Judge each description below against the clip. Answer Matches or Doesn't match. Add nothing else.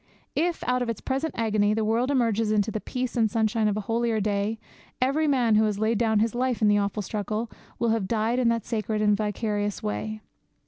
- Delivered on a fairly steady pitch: Matches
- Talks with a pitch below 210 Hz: Doesn't match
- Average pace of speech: Doesn't match